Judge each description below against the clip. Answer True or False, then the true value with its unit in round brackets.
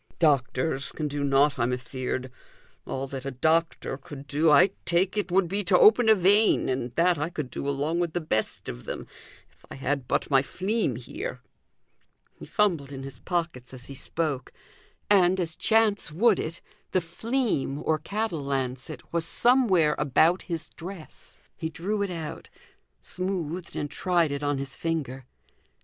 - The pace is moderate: True (170 wpm)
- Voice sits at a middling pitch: True (160 Hz)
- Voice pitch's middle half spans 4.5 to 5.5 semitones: True (4.9 semitones)